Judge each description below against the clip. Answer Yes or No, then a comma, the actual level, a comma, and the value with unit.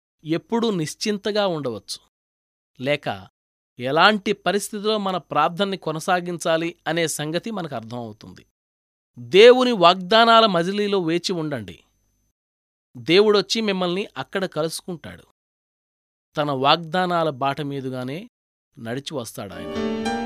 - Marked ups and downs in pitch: Yes, wide, 7.5 semitones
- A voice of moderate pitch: Yes, medium, 165 Hz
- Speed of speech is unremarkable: Yes, average, 80 wpm